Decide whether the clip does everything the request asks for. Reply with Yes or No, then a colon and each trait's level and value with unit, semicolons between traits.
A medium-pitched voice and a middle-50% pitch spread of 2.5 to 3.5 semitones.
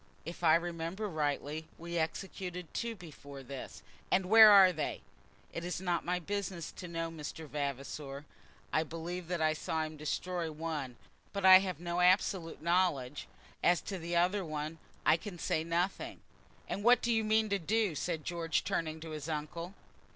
Yes: medium, 170 Hz; average, 2.9 semitones